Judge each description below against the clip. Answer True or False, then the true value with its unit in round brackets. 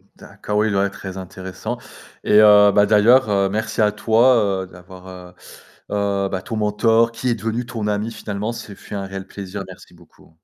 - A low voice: True (105 Hz)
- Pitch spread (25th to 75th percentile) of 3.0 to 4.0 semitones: False (2.5 semitones)